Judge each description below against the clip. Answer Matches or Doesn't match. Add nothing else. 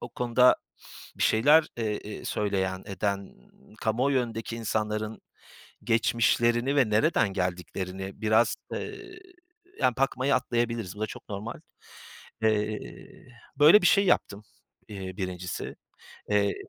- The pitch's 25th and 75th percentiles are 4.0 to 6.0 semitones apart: Doesn't match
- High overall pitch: Doesn't match